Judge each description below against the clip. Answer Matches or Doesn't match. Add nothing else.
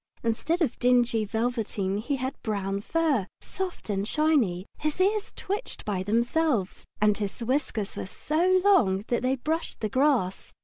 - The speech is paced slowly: Doesn't match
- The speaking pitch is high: Matches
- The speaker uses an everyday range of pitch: Doesn't match